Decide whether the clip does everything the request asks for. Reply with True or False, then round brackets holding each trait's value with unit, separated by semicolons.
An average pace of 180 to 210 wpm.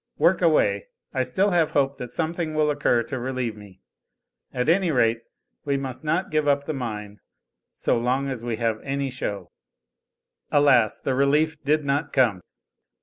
False (165 wpm)